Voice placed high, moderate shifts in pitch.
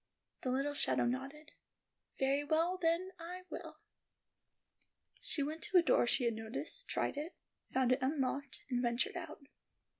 Yes: very high, 285 Hz; average, 4.2 semitones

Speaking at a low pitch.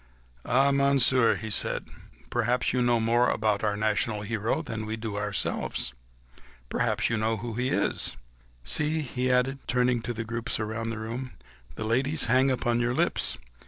Yes: low, 120 Hz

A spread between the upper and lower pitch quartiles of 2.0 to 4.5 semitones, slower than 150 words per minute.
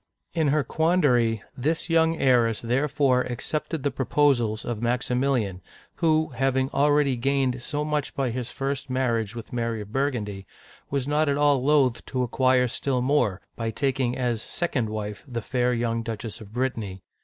No: average, 3.5 semitones; average, 160 wpm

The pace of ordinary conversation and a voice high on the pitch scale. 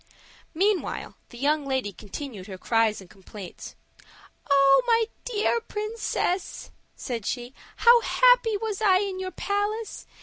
No: slow, 130 wpm; very high, 370 Hz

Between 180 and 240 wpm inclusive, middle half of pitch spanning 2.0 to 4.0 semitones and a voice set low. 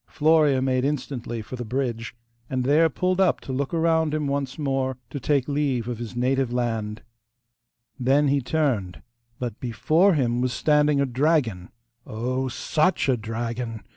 No: average, 160 wpm; average, 3.6 semitones; low, 130 Hz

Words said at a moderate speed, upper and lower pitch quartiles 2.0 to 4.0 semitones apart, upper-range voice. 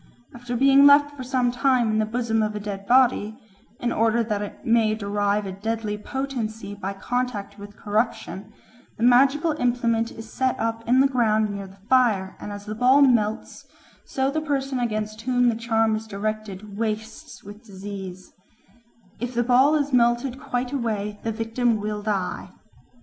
Yes: average, 170 wpm; average, 3.0 semitones; high, 225 Hz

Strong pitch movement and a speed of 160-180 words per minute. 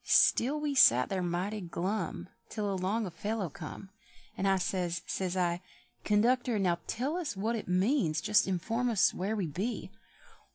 No: average, 4.0 semitones; average, 165 wpm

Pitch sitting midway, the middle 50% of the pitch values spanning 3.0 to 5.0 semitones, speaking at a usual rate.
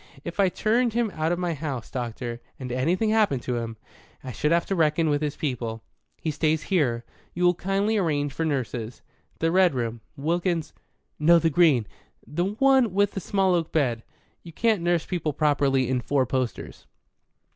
No: medium, 155 Hz; wide, 5.6 semitones; average, 180 wpm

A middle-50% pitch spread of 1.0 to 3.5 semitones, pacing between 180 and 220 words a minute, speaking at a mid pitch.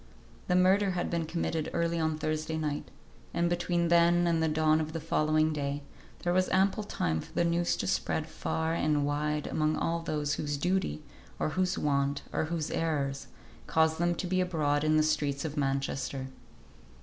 Yes: narrow, 2.5 semitones; average, 185 wpm; medium, 160 Hz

